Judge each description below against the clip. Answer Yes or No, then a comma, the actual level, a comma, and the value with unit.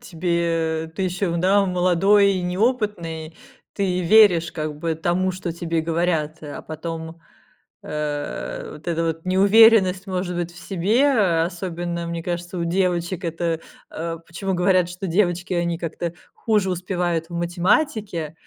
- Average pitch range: No, narrow, 2.2 semitones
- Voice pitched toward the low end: No, medium, 175 Hz